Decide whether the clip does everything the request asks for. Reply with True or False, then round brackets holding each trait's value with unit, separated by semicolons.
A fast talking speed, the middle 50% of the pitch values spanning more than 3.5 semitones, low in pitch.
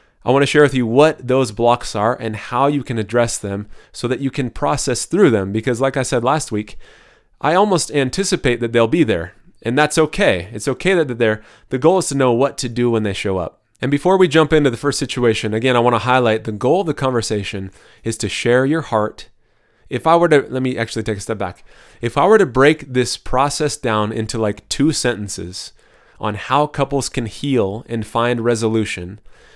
True (220 wpm; 4.3 semitones; 120 Hz)